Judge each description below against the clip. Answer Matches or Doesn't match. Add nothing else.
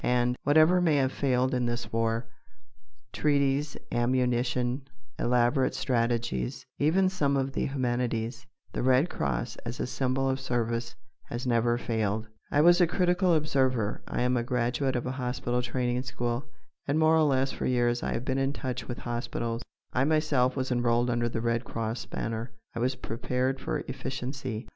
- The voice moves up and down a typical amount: Doesn't match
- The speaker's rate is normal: Matches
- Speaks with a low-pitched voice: Matches